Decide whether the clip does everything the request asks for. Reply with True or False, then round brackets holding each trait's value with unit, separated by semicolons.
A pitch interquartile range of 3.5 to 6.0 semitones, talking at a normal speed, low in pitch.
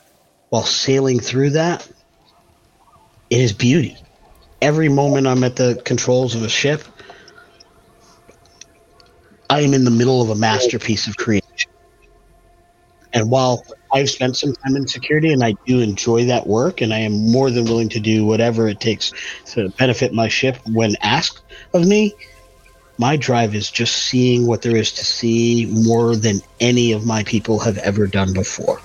False (2.9 semitones; 165 wpm; 120 Hz)